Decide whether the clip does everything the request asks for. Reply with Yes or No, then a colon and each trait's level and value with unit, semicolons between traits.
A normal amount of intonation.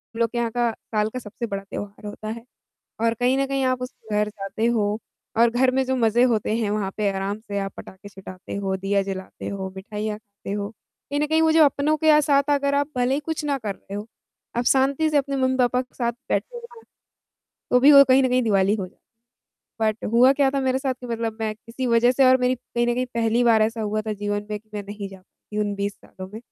Yes: average, 4.1 semitones